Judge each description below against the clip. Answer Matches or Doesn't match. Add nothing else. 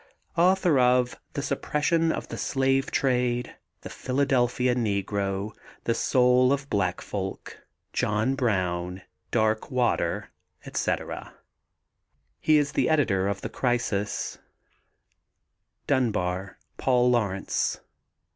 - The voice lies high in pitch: Doesn't match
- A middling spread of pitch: Matches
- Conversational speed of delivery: Doesn't match